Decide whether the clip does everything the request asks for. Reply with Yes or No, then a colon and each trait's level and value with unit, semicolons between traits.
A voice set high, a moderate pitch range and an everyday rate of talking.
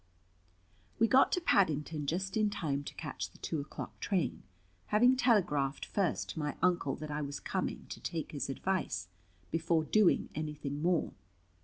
No: medium, 160 Hz; average, 4.7 semitones; average, 160 wpm